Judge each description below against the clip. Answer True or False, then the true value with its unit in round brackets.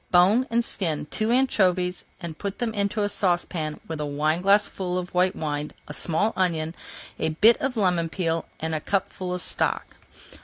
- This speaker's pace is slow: False (170 wpm)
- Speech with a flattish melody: False (4.0 semitones)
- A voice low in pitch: False (180 Hz)